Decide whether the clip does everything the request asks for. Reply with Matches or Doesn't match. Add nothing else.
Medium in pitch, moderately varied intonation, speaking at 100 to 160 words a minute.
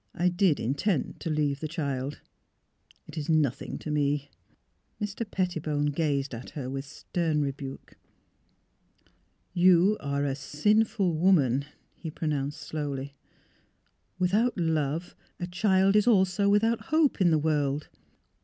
Matches